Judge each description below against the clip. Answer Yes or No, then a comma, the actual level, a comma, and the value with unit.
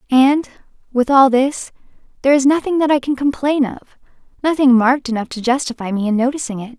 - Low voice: No, very high, 265 Hz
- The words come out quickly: No, average, 175 wpm